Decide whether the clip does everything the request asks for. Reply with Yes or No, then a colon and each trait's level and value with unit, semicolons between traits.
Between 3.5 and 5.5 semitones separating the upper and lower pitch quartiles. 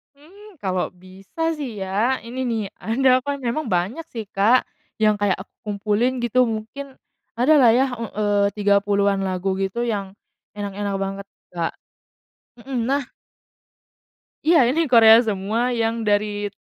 Yes: average, 4.0 semitones